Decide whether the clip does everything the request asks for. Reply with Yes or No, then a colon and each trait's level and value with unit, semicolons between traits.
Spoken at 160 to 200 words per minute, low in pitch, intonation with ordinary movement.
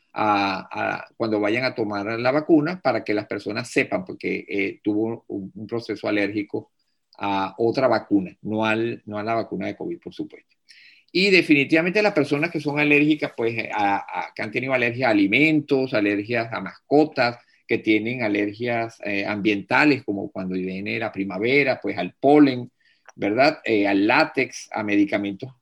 No: average, 165 wpm; low, 115 Hz; wide, 5.7 semitones